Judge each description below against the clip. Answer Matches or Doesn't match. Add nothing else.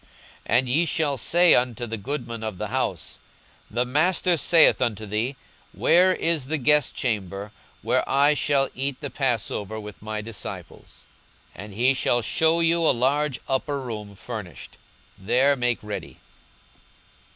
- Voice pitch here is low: Matches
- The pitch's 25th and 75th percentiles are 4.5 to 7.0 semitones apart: Matches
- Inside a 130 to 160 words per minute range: Matches